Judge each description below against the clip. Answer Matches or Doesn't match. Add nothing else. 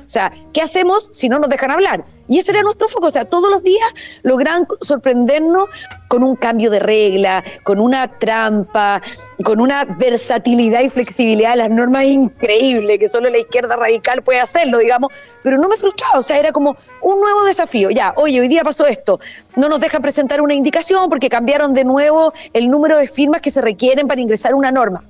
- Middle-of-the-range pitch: Doesn't match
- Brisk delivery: Matches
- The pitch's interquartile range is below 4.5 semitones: Doesn't match